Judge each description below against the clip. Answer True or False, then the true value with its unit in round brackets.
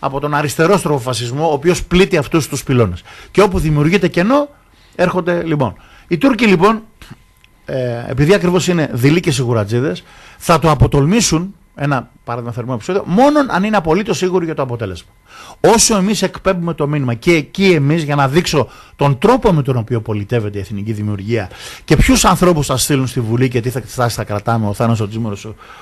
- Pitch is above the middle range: False (145 Hz)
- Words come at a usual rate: False (180 wpm)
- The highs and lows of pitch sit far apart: True (7.0 semitones)